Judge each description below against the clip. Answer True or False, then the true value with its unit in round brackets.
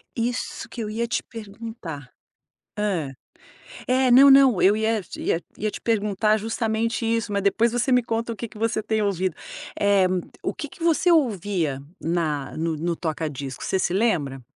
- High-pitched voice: True (210 Hz)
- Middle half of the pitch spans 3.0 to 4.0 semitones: False (4.8 semitones)